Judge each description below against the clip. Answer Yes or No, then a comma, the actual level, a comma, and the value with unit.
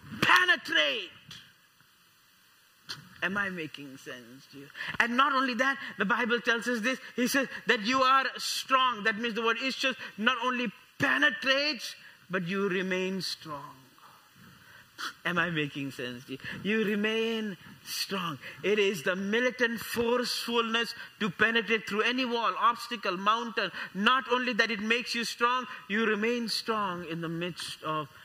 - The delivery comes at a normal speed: Yes, average, 150 wpm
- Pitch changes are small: No, average, 4.6 semitones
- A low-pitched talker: No, high, 225 Hz